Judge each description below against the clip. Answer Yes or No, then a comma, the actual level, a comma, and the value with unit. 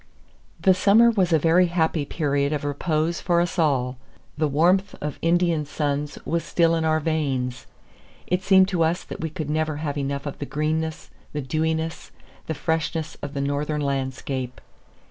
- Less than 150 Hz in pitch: No, medium, 155 Hz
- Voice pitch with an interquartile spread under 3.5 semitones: Yes, average, 2.7 semitones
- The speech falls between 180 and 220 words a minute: No, average, 170 wpm